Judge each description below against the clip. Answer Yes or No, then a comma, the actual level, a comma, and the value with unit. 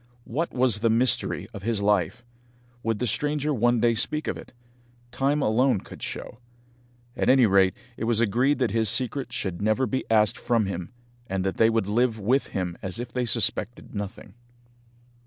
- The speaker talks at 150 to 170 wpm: No, average, 180 wpm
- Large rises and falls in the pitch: No, average, 3.5 semitones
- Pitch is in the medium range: No, low, 115 Hz